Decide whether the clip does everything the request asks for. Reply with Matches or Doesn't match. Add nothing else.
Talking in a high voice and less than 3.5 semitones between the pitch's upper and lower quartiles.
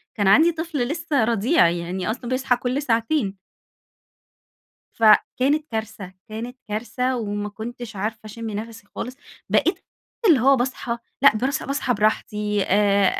Doesn't match